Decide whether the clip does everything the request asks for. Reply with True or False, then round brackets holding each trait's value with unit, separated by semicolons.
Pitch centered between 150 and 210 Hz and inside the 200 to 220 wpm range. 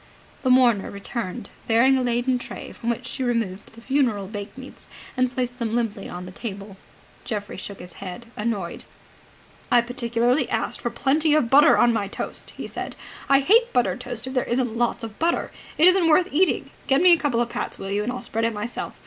False (240 Hz; 205 wpm)